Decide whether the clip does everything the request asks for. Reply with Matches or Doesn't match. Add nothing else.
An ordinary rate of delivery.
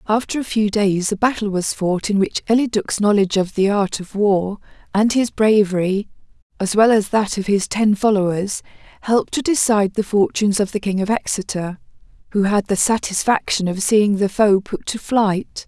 Matches